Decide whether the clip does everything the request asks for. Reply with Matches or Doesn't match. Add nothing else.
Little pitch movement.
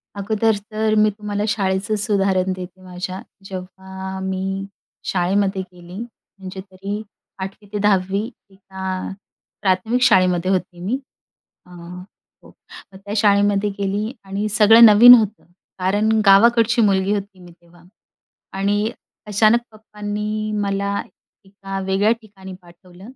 Matches